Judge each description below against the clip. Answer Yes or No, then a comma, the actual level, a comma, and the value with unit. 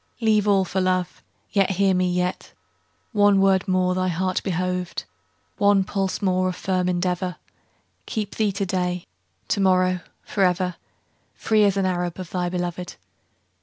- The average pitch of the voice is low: No, medium, 185 Hz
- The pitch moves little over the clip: Yes, narrow, 1.3 semitones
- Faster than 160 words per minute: No, average, 150 wpm